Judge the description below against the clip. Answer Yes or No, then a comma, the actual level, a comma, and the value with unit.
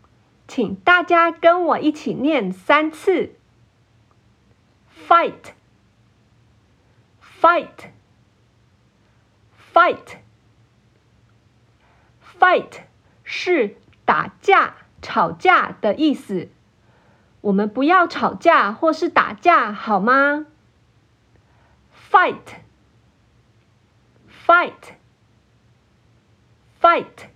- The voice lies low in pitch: Yes, low, 120 Hz